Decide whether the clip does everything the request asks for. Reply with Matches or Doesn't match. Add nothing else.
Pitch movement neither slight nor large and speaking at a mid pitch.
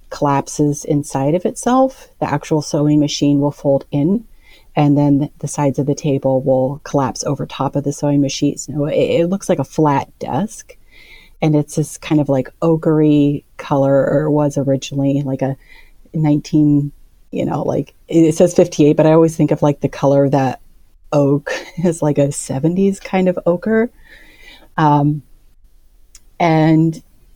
Doesn't match